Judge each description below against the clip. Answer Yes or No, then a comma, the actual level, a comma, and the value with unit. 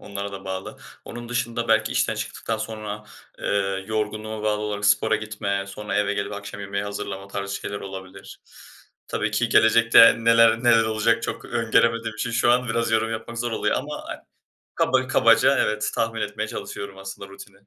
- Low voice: Yes, low, 105 Hz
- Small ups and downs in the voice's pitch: Yes, narrow, 2.2 semitones